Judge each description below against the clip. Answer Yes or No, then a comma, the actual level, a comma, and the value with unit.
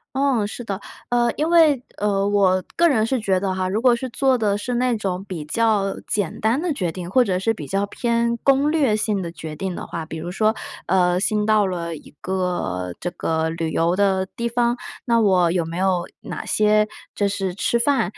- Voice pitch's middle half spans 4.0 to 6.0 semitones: Yes, average, 4.5 semitones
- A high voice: Yes, high, 200 Hz